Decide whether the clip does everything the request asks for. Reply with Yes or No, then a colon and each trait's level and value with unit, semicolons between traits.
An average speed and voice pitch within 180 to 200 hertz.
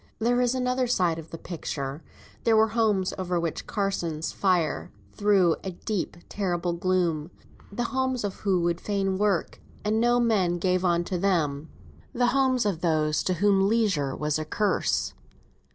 Yes: average, 165 wpm; high, 190 Hz